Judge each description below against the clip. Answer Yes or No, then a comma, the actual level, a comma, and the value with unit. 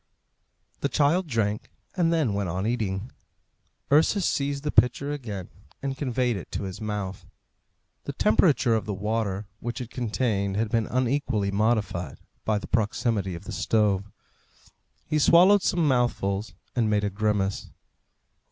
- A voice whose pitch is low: Yes, low, 110 Hz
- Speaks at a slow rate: No, average, 145 wpm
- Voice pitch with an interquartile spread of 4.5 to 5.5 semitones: Yes, average, 4.9 semitones